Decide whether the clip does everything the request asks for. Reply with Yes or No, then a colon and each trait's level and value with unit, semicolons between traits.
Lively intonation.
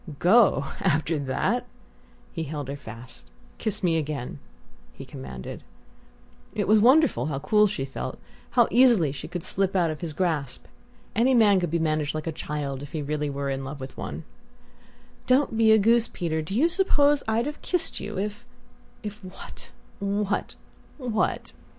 Yes: wide, 7.0 semitones